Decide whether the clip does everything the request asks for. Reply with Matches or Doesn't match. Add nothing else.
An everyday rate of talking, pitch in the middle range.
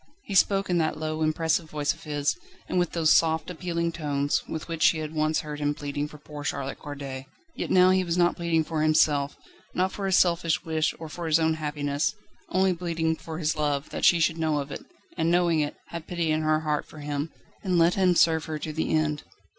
Doesn't match